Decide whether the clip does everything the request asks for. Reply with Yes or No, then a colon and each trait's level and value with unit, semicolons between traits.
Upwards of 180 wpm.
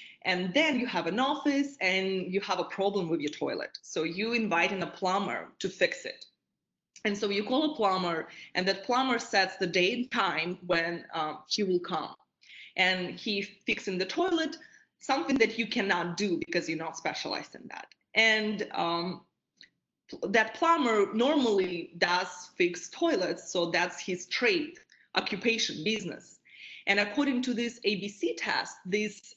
No: average, 160 wpm